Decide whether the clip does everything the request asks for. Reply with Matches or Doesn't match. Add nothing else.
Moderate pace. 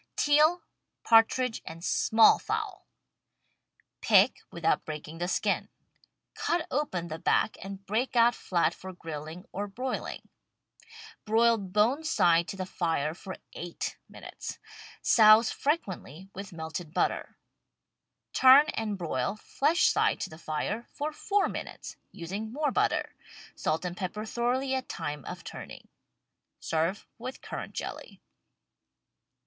Doesn't match